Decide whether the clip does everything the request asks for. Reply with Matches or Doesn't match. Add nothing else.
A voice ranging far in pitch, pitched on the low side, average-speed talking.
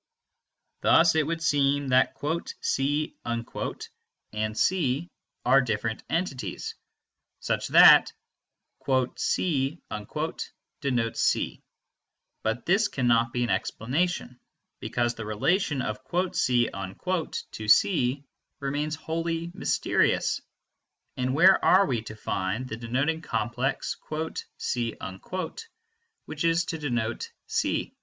Doesn't match